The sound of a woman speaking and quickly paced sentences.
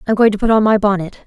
Yes: female; fast, 380 wpm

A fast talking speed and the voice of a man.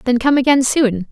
No: fast, 215 wpm; female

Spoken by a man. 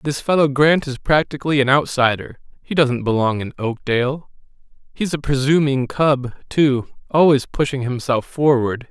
Yes: male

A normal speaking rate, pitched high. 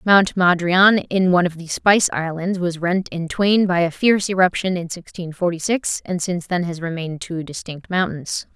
No: average, 195 wpm; medium, 180 Hz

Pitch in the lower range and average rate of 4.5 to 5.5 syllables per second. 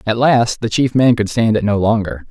Yes: low, 110 Hz; 5.1 syllables/s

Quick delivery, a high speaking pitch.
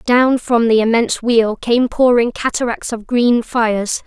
No: average, 160 wpm; high, 235 Hz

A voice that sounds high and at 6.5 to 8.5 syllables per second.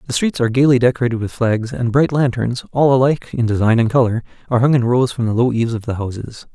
No: low, 120 Hz; 6.7 syllables/s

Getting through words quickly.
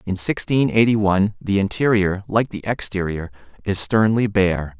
No: average, 150 wpm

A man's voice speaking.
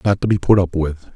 Yes: male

